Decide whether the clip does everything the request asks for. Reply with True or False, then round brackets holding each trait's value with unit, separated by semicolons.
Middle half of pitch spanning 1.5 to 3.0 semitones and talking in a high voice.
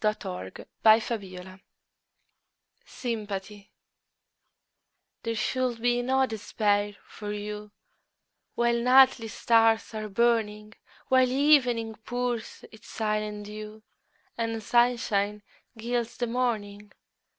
True (2.4 semitones; 225 Hz)